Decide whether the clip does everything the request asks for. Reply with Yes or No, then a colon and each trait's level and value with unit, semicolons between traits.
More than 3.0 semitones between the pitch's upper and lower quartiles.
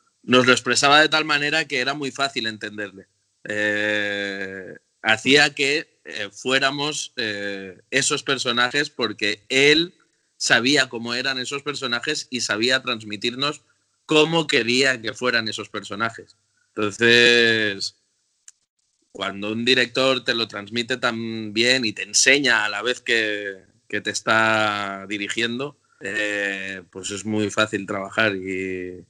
Yes: average, 4.4 semitones